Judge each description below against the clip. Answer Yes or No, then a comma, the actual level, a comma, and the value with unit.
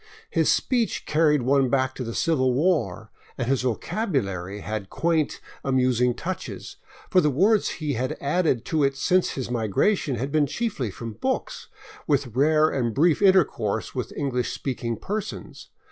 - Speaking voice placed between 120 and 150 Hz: Yes, low, 135 Hz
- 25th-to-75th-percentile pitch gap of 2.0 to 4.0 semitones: No, average, 5.0 semitones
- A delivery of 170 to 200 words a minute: No, average, 155 wpm